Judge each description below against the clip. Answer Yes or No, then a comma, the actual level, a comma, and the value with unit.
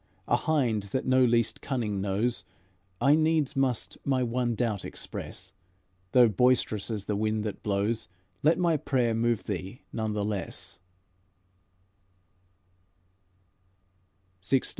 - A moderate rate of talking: No, slow, 120 wpm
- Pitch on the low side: Yes, low, 115 Hz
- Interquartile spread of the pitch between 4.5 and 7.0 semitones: No, average, 3.6 semitones